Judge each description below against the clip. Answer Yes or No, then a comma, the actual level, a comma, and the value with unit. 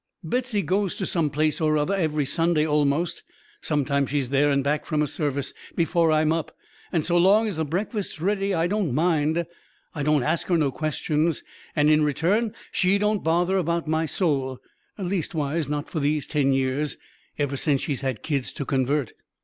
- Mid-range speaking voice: Yes, medium, 155 Hz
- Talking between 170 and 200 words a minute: Yes, average, 180 wpm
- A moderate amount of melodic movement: Yes, average, 3.1 semitones